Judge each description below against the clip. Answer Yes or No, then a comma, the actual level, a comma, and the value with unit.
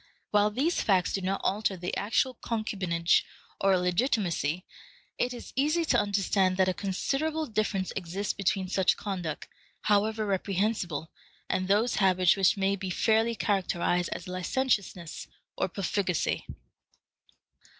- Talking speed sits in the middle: No, slow, 130 wpm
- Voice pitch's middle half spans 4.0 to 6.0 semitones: No, average, 2.9 semitones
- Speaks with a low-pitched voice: No, high, 195 Hz